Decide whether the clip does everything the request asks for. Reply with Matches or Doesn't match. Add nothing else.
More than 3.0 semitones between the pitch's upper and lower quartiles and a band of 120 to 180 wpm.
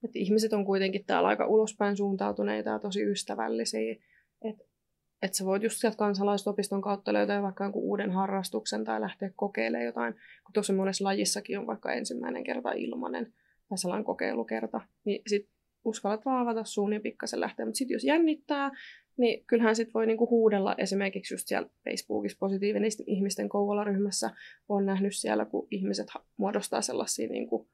Doesn't match